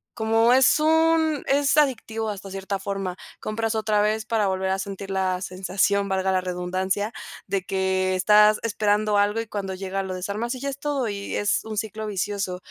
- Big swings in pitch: No, average, 2.7 semitones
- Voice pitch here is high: Yes, high, 205 Hz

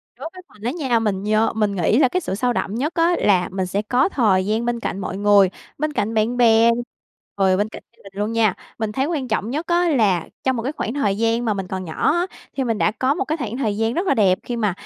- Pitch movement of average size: Yes, average, 4.4 semitones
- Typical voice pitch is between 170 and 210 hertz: No, high, 225 Hz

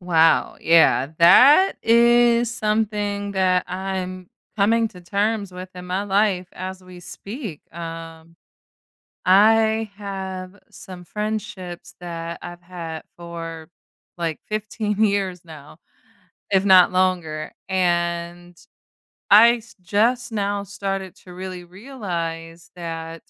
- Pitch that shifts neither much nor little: Yes, average, 3.3 semitones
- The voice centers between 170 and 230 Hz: Yes, medium, 185 Hz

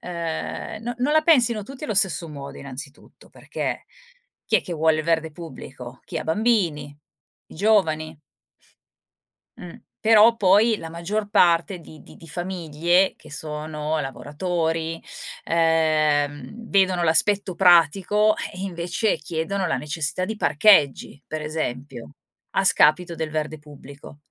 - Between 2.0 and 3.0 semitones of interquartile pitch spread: No, average, 4.3 semitones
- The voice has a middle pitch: Yes, medium, 165 Hz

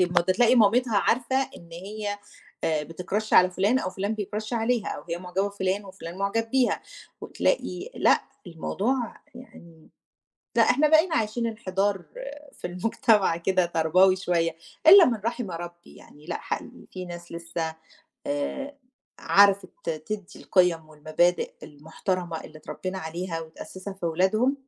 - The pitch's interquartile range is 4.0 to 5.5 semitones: Yes, average, 4.6 semitones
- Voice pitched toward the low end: No, high, 190 Hz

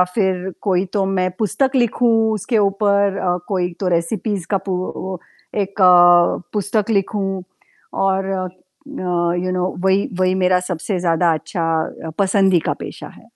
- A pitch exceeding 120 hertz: Yes, high, 190 Hz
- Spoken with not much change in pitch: Yes, narrow, 1.8 semitones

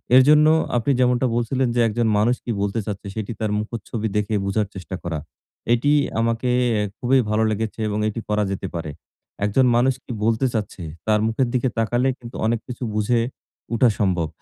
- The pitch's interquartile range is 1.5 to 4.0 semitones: Yes, average, 2.7 semitones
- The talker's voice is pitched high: No, low, 115 Hz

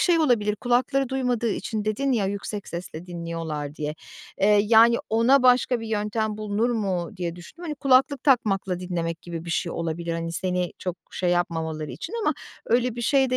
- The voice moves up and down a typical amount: No, wide, 6.2 semitones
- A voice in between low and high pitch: No, high, 210 Hz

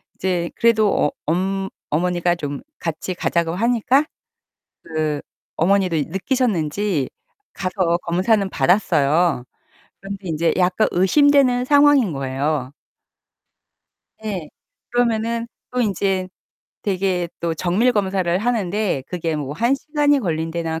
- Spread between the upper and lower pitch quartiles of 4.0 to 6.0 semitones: Yes, average, 5.1 semitones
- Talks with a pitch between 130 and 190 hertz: Yes, medium, 185 Hz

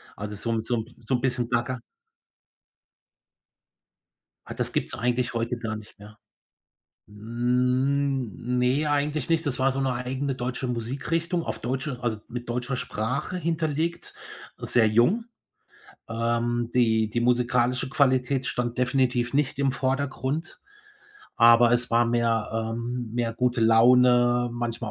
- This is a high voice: No, low, 125 Hz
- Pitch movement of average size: No, narrow, 2.1 semitones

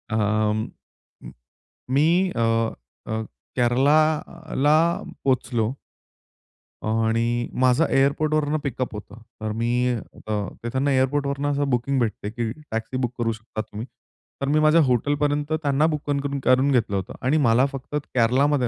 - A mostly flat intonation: No, average, 4.0 semitones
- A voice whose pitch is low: Yes, low, 130 Hz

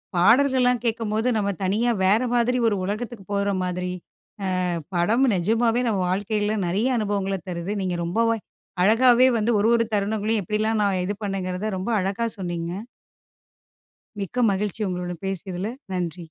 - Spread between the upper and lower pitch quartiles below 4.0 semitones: Yes, average, 3.6 semitones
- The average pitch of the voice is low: No, high, 205 Hz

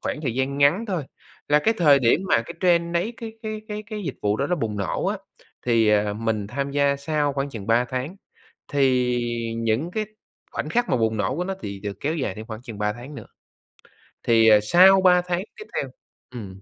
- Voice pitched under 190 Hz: Yes, medium, 140 Hz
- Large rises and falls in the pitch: Yes, wide, 7.6 semitones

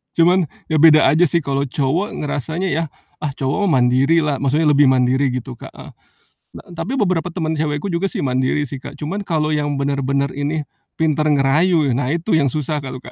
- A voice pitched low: No, medium, 150 Hz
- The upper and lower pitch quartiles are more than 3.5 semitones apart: No, average, 3.0 semitones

